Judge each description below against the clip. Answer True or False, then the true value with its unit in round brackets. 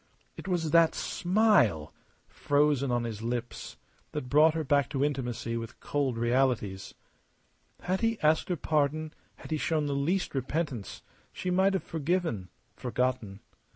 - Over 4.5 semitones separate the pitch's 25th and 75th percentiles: True (5.1 semitones)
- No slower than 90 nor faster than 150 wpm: True (145 wpm)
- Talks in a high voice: False (145 Hz)